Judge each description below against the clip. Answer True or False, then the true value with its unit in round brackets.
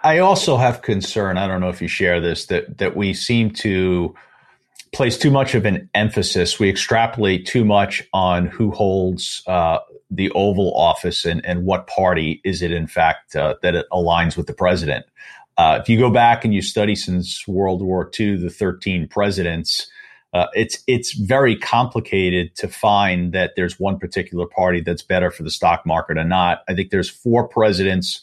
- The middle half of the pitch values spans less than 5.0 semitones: True (3.4 semitones)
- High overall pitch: False (95 Hz)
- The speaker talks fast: False (185 wpm)